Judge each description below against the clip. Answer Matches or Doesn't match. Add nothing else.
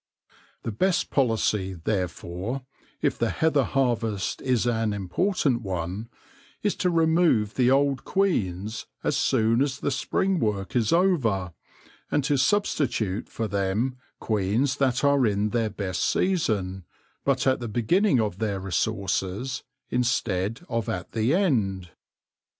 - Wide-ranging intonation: Matches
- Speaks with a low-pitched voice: Matches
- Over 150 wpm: Doesn't match